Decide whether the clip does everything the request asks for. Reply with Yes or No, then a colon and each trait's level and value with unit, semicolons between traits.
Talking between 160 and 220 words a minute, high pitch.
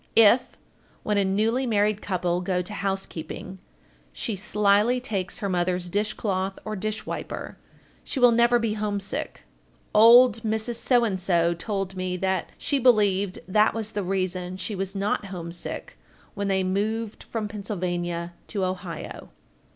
No: average, 140 wpm; high, 200 Hz